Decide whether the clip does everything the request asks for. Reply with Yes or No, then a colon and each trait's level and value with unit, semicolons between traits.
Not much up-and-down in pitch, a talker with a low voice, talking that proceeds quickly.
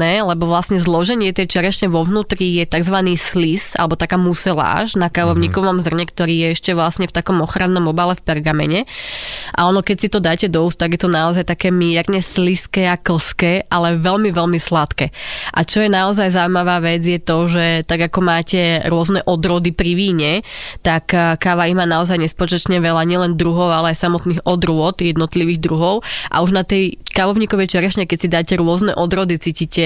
No: narrow, 1.8 semitones; medium, 175 Hz; fast, 180 wpm